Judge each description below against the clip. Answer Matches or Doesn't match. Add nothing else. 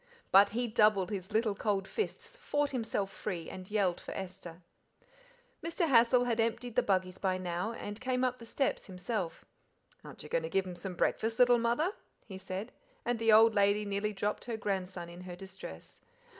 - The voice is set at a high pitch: Matches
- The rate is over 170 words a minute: Matches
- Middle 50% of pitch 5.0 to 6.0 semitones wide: Doesn't match